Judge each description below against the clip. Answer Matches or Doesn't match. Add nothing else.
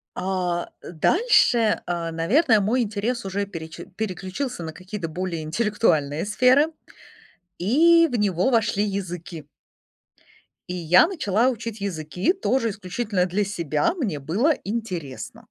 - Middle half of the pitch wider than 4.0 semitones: Matches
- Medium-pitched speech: Doesn't match